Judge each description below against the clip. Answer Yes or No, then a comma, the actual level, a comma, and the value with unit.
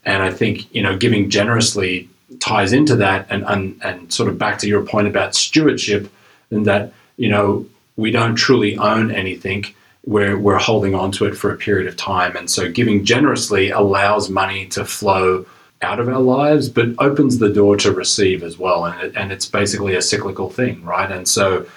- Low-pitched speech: Yes, low, 100 Hz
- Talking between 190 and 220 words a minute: Yes, average, 200 wpm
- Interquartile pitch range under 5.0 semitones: Yes, narrow, 2.6 semitones